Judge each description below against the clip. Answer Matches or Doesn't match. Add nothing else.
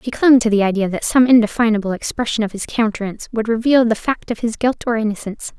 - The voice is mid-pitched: Doesn't match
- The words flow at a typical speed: Doesn't match